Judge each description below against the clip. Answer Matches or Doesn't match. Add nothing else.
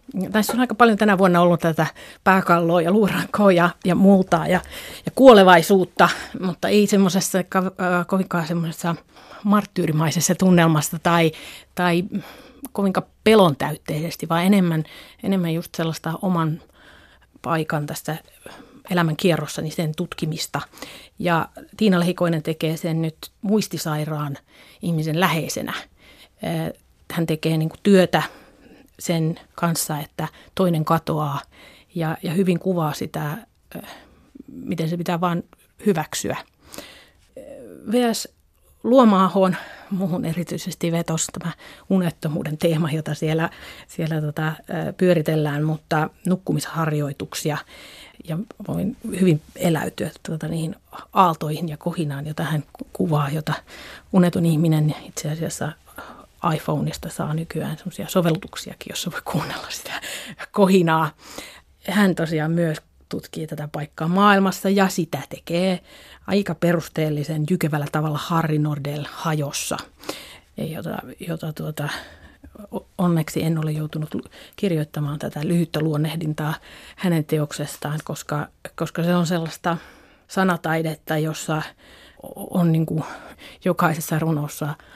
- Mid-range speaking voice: Matches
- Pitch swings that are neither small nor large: Matches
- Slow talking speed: Doesn't match